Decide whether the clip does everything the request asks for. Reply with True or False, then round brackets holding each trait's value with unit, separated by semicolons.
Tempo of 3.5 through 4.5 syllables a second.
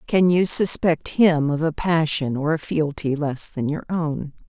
True (4.1 syllables/s)